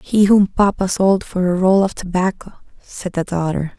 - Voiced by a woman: Yes, female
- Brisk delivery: No, average, 190 wpm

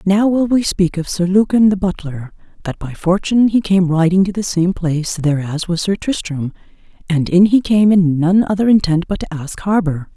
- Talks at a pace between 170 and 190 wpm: No, fast, 205 wpm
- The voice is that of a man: No, female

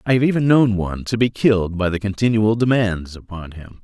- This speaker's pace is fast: Yes, fast, 220 wpm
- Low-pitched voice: Yes, low, 105 Hz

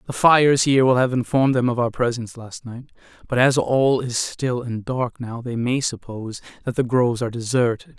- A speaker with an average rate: No, fast, 210 wpm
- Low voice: Yes, low, 125 Hz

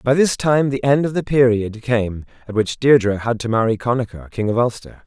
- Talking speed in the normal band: No, fast, 225 wpm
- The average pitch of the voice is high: No, low, 120 Hz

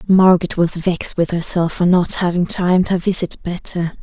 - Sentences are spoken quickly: No, average, 180 wpm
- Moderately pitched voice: Yes, medium, 175 Hz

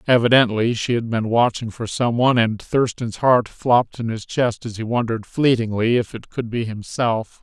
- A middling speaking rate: Yes, average, 195 wpm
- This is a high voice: No, low, 115 Hz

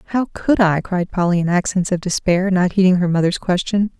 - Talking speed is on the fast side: Yes, fast, 210 wpm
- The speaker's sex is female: Yes, female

